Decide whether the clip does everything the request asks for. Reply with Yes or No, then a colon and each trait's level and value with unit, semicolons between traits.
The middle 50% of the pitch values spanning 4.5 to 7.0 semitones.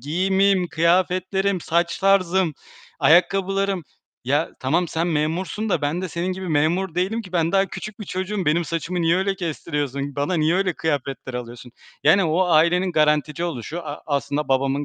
No: average, 3.7 semitones